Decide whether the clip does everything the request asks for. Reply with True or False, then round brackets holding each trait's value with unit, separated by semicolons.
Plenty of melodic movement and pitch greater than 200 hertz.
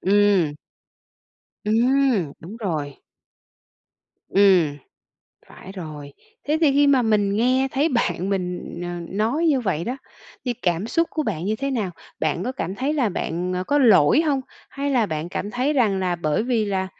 True (6.6 semitones; 210 Hz)